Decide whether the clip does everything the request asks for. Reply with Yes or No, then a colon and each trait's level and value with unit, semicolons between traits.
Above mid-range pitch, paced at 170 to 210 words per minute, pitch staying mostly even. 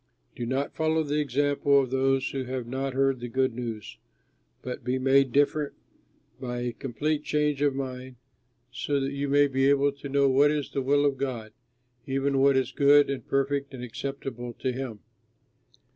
No: low, 135 Hz; average, 180 wpm; narrow, 1.6 semitones